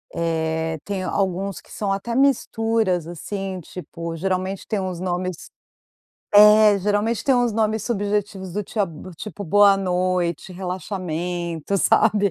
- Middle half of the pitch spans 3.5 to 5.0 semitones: No, average, 2.7 semitones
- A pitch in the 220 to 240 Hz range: No, high, 195 Hz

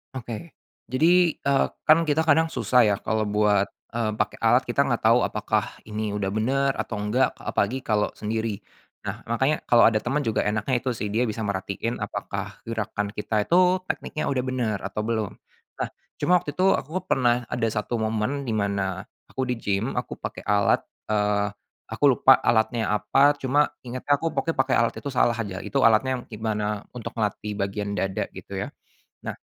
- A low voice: Yes, low, 115 Hz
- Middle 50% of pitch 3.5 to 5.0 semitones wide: Yes, average, 4.0 semitones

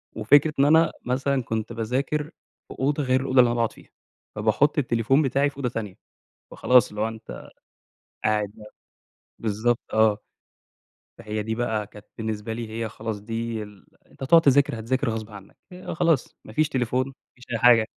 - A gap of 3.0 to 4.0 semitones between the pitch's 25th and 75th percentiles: Yes, average, 3.6 semitones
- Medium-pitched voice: No, low, 115 Hz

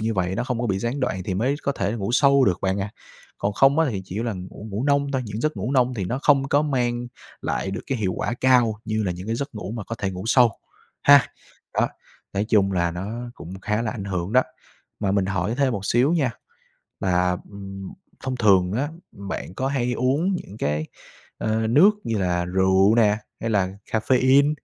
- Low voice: Yes, low, 110 Hz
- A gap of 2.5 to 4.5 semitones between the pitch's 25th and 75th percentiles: No, average, 4.9 semitones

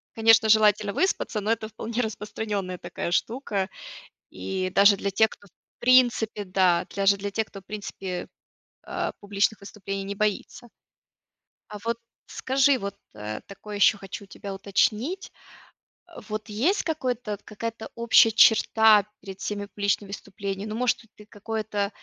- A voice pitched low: No, high, 210 Hz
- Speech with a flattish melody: Yes, narrow, 2.1 semitones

